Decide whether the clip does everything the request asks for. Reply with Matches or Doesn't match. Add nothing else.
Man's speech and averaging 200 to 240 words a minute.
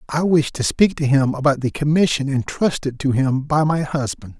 Matches